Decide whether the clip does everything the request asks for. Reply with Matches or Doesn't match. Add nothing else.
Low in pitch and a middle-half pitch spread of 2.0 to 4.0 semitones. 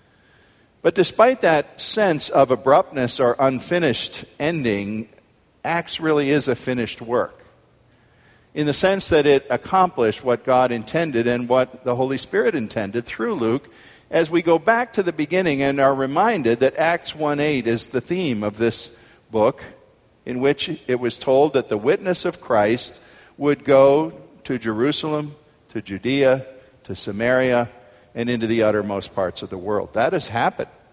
Doesn't match